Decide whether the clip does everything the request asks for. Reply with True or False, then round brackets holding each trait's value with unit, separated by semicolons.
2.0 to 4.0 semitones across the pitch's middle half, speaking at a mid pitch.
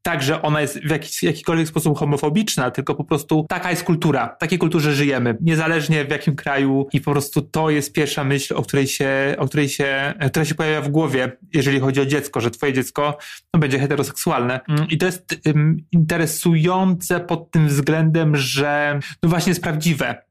True (2.5 semitones; 150 Hz)